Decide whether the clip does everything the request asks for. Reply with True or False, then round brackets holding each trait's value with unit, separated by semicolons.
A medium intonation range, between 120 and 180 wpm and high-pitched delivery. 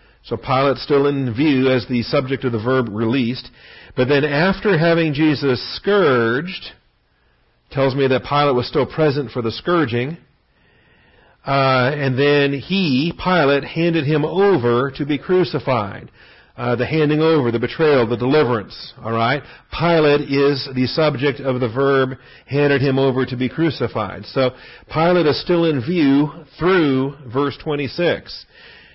False (3.4 semitones; 145 wpm; 140 Hz)